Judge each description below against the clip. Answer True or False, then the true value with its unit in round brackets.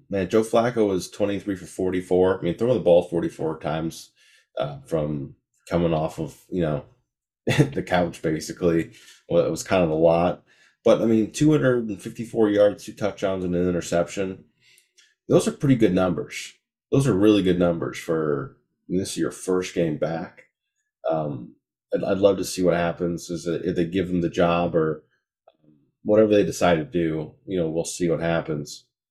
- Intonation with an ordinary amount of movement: True (3.3 semitones)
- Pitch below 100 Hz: True (90 Hz)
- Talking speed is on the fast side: False (185 wpm)